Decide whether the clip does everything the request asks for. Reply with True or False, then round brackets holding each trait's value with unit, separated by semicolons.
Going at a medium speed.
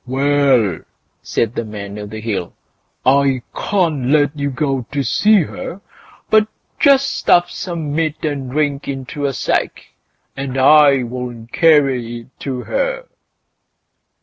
False (130 wpm)